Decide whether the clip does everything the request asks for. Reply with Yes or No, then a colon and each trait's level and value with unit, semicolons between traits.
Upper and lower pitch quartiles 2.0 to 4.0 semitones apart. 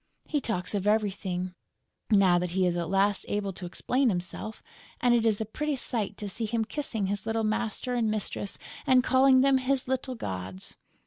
No: average, 4.6 semitones